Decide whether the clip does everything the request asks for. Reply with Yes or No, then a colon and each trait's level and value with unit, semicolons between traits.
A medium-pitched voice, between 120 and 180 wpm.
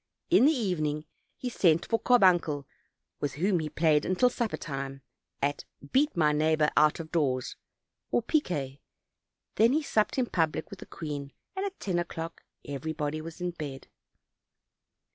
Yes: medium, 160 Hz; average, 160 wpm